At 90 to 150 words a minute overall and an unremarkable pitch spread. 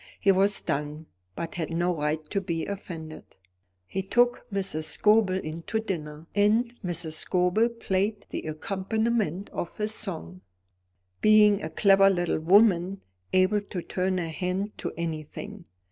Yes: average, 145 wpm; average, 4.0 semitones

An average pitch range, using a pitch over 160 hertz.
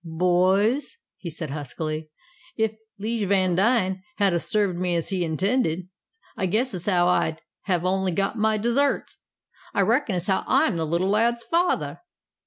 Yes: average, 4.1 semitones; high, 190 Hz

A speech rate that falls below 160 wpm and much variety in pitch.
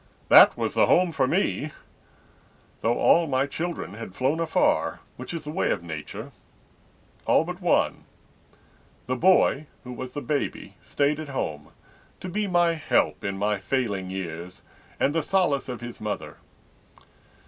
Yes: average, 150 wpm; wide, 7.6 semitones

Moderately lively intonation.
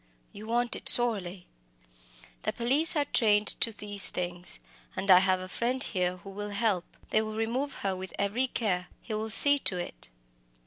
Yes: average, 4.1 semitones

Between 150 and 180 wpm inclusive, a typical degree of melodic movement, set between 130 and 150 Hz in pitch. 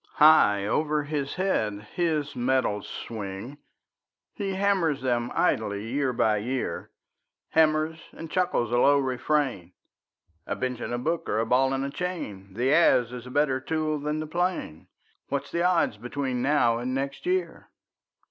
Yes: average, 155 wpm; average, 4.6 semitones; low, 135 Hz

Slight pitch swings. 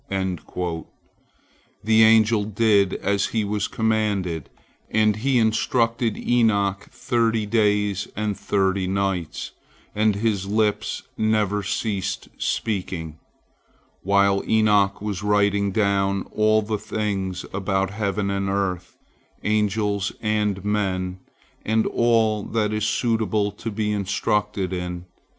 Yes: narrow, 1.9 semitones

